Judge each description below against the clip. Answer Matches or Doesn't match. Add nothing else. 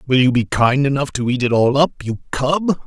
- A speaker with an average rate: Doesn't match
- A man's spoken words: Matches